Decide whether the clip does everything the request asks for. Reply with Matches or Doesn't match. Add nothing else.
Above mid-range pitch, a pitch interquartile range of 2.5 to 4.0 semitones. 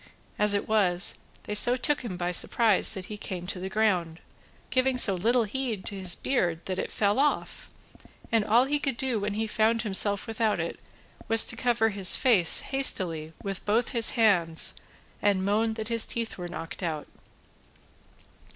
Matches